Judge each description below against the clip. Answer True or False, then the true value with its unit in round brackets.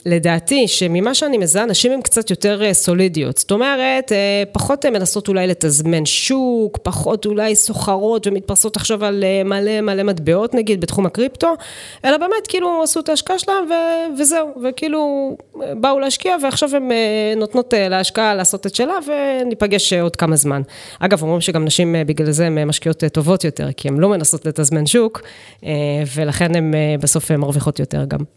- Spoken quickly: True (155 wpm)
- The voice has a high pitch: True (200 Hz)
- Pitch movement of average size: False (7.5 semitones)